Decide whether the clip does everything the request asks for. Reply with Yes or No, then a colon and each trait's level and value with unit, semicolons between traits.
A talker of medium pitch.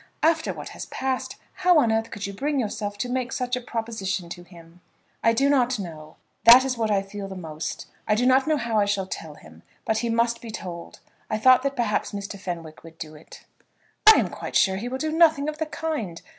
No: high, 225 Hz